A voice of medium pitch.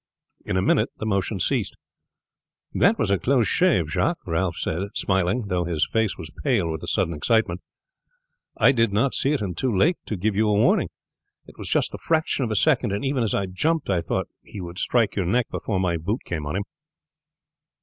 No: low, 100 Hz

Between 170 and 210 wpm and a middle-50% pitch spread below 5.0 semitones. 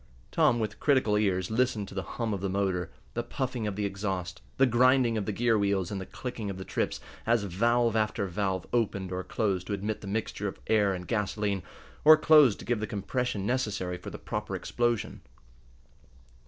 Yes: average, 195 wpm; average, 3.4 semitones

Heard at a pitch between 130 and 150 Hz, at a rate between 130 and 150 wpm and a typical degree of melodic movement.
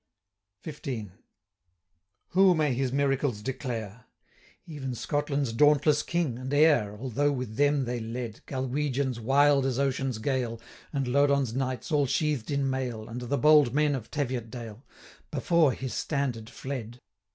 Yes: low, 135 Hz; average, 140 wpm; average, 3.2 semitones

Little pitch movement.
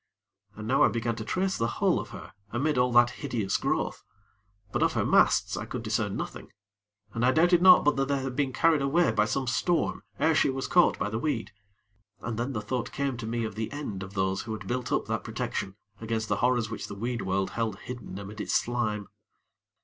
No: average, 4.1 semitones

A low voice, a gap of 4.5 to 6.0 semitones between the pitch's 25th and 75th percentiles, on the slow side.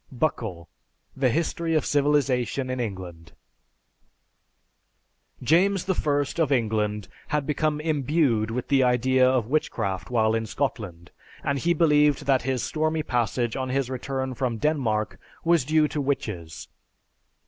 Yes: low, 130 Hz; average, 4.9 semitones; slow, 130 wpm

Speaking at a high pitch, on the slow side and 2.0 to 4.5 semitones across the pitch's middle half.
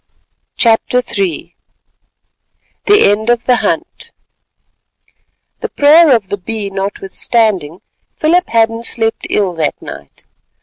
Yes: high, 225 Hz; slow, 105 wpm; average, 3.6 semitones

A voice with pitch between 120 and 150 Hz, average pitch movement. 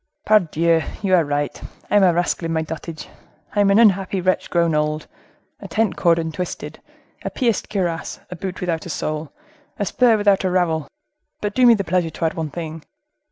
No: medium, 175 Hz; average, 3.6 semitones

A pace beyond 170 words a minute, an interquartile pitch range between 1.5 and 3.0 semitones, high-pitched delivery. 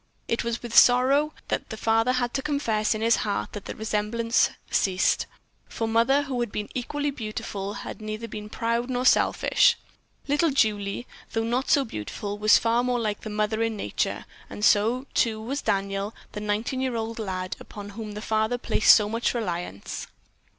Yes: average, 185 wpm; narrow, 2.6 semitones; high, 225 Hz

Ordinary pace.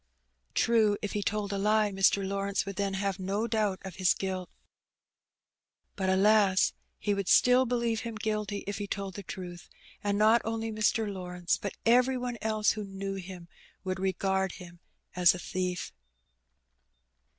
Yes: average, 160 wpm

